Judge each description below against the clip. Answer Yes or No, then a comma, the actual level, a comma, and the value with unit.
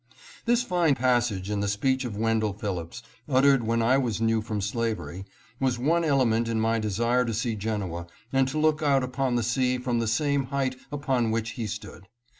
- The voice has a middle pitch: No, low, 120 Hz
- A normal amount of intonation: Yes, average, 3.4 semitones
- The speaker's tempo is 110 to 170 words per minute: No, average, 195 wpm